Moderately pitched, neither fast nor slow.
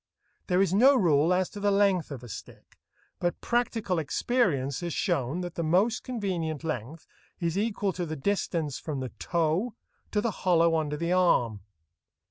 Yes: medium, 175 Hz; average, 170 wpm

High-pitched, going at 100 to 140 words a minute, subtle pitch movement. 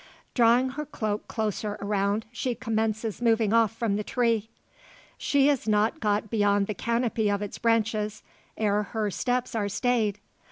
No: high, 220 Hz; average, 155 wpm; narrow, 2.1 semitones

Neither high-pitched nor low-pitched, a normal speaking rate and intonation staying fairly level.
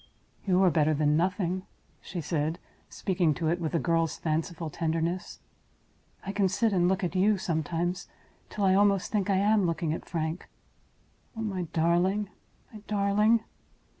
No: medium, 180 Hz; average, 160 wpm; average, 3.2 semitones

